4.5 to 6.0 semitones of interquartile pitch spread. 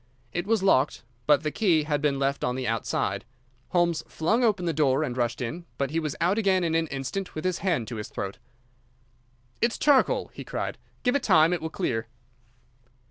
Yes: wide, 5.4 semitones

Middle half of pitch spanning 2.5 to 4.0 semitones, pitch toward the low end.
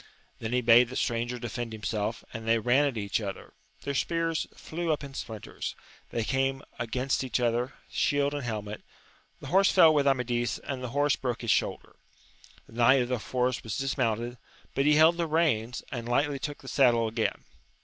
Yes: average, 3.4 semitones; low, 125 Hz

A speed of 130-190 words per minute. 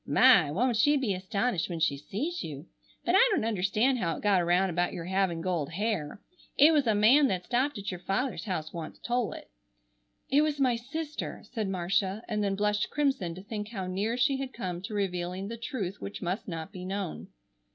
No: fast, 205 wpm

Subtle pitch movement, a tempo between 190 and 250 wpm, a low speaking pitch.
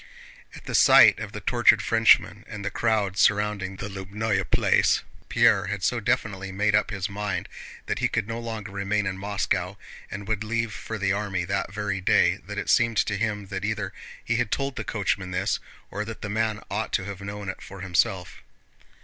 Yes: narrow, 1.9 semitones; average, 200 wpm; low, 100 Hz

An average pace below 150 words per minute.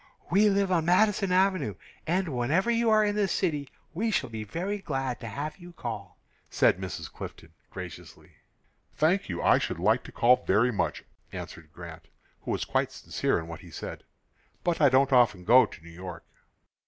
No: average, 185 wpm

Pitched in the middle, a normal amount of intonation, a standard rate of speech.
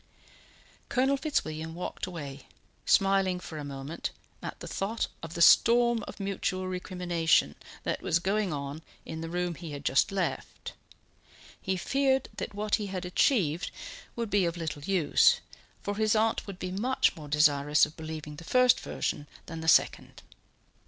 Yes: medium, 180 Hz; average, 4.6 semitones; average, 160 wpm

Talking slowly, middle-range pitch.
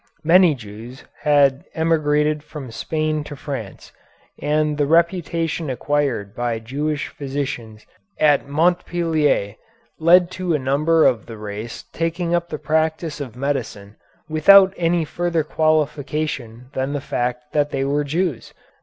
Yes: slow, 130 wpm; medium, 150 Hz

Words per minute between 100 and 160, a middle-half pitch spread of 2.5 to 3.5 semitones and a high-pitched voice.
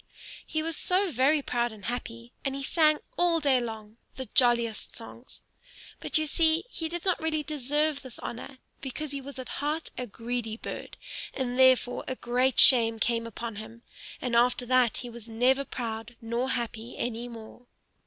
No: average, 175 wpm; average, 3.2 semitones; very high, 250 Hz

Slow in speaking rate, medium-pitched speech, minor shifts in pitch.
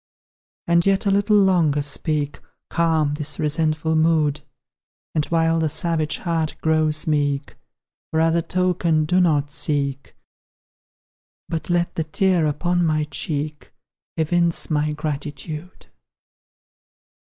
Yes: slow, 115 wpm; medium, 160 Hz; narrow, 2.1 semitones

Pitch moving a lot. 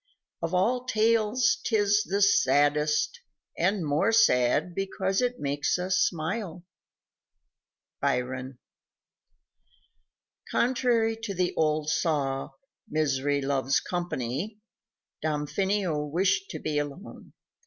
Yes: wide, 5.9 semitones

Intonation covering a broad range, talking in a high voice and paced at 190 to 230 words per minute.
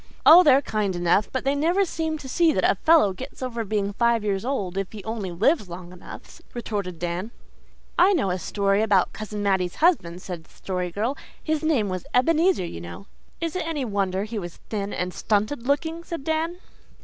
Yes: wide, 7.9 semitones; high, 215 Hz; fast, 205 wpm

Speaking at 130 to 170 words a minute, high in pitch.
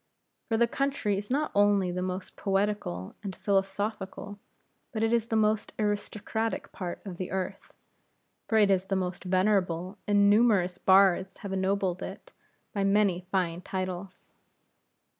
Yes: average, 145 wpm; high, 195 Hz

